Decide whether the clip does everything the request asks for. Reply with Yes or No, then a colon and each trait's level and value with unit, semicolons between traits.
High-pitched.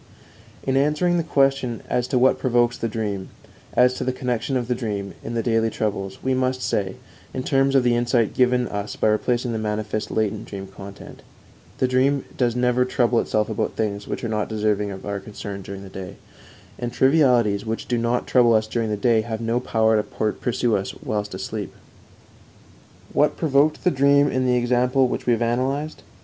No: low, 120 Hz